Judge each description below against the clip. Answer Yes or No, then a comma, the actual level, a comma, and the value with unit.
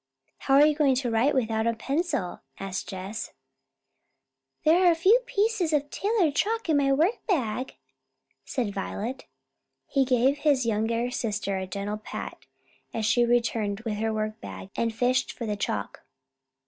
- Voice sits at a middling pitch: No, high, 245 Hz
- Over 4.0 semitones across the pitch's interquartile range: Yes, wide, 5.4 semitones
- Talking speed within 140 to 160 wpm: Yes, average, 145 wpm